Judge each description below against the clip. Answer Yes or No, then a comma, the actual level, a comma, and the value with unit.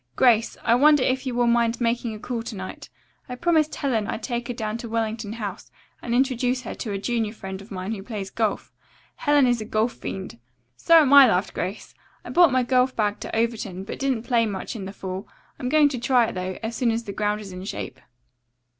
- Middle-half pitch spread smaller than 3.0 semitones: No, average, 3.3 semitones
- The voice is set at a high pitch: Yes, high, 230 Hz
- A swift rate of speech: Yes, fast, 230 wpm